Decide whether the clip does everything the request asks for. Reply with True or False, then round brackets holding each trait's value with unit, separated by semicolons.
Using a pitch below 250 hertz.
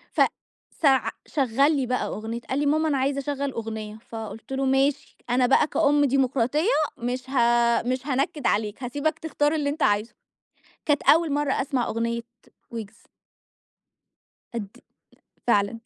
False (265 Hz)